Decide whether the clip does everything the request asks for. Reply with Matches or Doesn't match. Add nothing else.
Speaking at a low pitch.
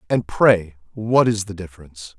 Matches